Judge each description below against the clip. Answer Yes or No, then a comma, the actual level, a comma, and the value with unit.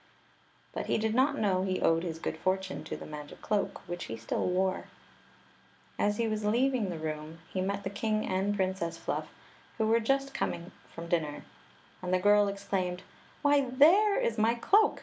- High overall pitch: Yes, high, 195 Hz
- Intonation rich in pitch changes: No, average, 4.2 semitones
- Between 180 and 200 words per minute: Yes, average, 185 wpm